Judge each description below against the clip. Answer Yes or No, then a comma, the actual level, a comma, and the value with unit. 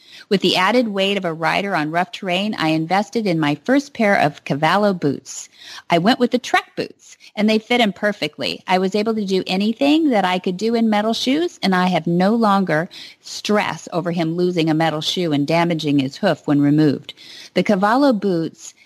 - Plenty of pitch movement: No, average, 4.9 semitones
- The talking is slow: No, fast, 205 wpm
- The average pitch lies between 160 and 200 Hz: Yes, high, 190 Hz